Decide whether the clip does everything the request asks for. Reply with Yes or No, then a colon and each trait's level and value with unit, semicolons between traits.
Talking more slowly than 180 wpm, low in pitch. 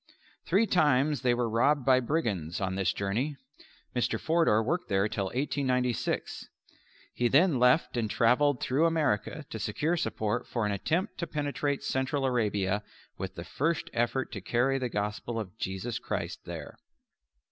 Yes: average, 155 wpm; low, 125 Hz